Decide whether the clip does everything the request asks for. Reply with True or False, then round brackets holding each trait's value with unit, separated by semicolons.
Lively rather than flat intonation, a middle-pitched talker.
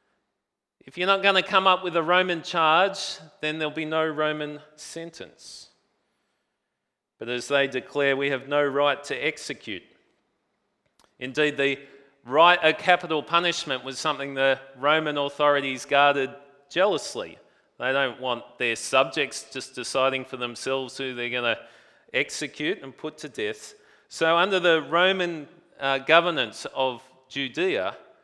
False (3.9 semitones; 150 Hz)